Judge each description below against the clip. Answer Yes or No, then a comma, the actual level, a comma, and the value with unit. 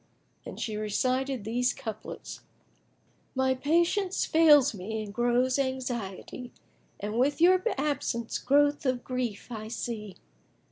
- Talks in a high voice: Yes, very high, 250 Hz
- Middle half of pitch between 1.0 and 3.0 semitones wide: No, average, 4.1 semitones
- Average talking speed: No, slow, 125 wpm